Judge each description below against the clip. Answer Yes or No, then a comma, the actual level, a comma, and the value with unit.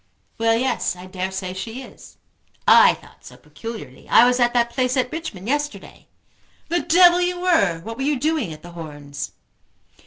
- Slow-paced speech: No, average, 180 wpm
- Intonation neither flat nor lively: No, wide, 7.9 semitones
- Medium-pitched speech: No, high, 235 Hz